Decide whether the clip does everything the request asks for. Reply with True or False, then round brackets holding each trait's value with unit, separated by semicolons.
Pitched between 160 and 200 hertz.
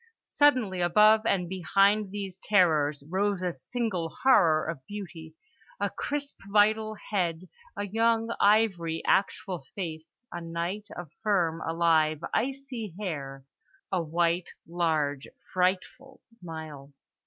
True (185 Hz)